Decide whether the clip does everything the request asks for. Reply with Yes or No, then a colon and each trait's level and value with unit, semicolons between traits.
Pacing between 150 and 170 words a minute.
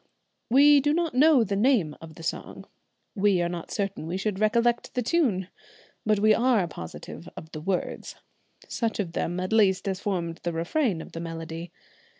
No: average, 180 wpm